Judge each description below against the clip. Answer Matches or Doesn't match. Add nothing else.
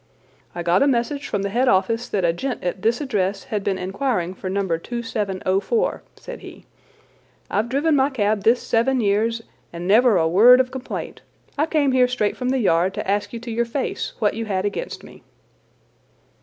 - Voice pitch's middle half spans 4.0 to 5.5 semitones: Matches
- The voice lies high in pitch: Matches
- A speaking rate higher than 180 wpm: Matches